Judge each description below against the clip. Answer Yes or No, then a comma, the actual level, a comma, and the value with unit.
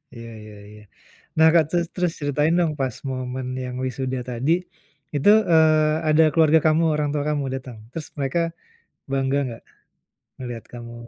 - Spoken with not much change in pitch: No, average, 3.8 semitones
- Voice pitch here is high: No, medium, 140 Hz